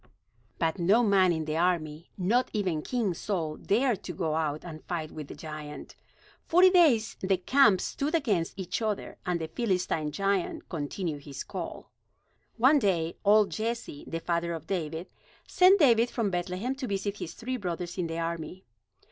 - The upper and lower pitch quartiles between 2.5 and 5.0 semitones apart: No, wide, 5.4 semitones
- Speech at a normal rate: Yes, average, 170 wpm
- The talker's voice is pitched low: No, medium, 185 Hz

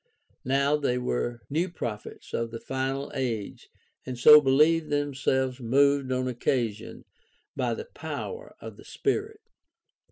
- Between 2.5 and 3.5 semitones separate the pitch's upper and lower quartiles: Yes, average, 3.2 semitones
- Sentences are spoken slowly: Yes, slow, 130 wpm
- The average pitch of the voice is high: No, low, 135 Hz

